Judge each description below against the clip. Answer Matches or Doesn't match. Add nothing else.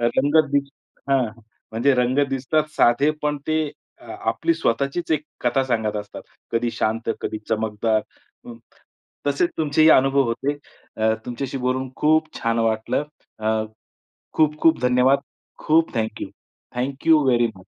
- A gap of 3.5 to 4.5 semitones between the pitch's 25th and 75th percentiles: Matches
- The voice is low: Matches